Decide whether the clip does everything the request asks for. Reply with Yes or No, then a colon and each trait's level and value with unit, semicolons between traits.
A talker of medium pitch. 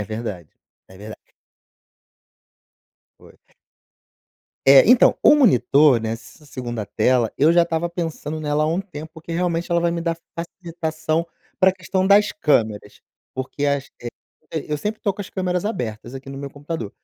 Yes: medium, 155 Hz